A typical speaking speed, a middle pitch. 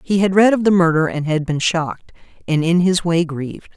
No: fast, 240 wpm; medium, 170 Hz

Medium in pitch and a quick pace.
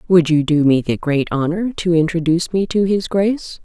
Yes: medium, 170 Hz; fast, 215 wpm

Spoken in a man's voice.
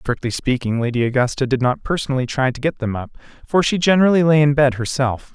Yes: male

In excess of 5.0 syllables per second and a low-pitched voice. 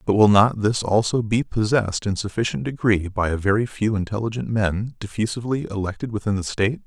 Yes: 5.8 syllables/s; low, 105 Hz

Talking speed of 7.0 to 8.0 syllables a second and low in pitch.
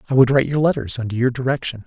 Yes: 7.8 syllables/s; low, 125 Hz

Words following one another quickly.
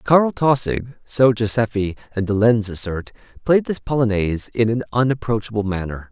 No: average, 145 wpm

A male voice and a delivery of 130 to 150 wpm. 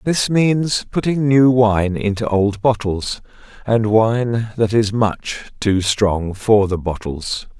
Yes: male; average, 140 wpm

